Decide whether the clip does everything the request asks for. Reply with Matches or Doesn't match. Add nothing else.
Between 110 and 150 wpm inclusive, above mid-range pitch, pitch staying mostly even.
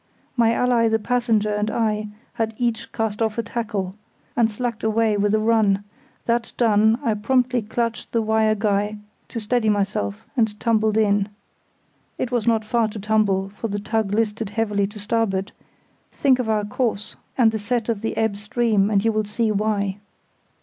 Doesn't match